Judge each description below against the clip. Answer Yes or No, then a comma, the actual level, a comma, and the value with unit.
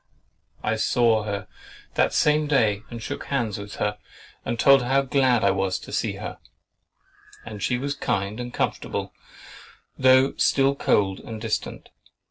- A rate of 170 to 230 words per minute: No, average, 155 wpm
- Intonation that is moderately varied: Yes, average, 4.4 semitones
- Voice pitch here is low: Yes, low, 115 Hz